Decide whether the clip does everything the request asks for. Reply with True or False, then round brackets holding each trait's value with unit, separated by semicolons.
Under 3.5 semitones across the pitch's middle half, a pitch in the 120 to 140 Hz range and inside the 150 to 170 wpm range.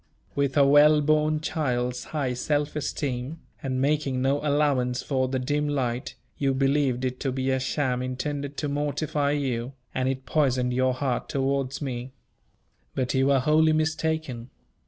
True (2.4 semitones; 135 Hz; 155 wpm)